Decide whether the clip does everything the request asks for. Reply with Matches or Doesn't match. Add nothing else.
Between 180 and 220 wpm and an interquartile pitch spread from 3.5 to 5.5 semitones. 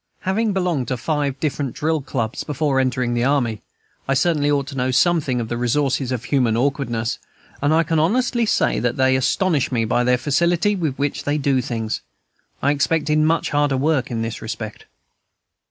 Matches